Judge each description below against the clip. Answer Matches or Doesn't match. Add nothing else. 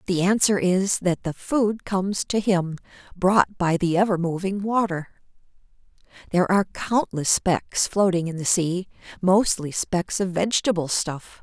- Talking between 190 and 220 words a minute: Doesn't match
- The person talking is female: Matches